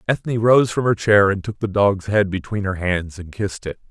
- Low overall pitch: Yes, low, 100 Hz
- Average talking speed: No, fast, 245 wpm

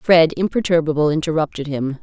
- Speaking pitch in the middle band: Yes, medium, 160 Hz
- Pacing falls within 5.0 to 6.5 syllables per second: Yes, 5.5 syllables/s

